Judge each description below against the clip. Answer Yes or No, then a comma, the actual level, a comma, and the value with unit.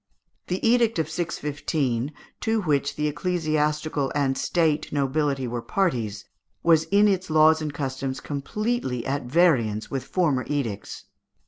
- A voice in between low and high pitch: Yes, medium, 150 Hz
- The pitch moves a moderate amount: Yes, average, 4.1 semitones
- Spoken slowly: Yes, slow, 130 wpm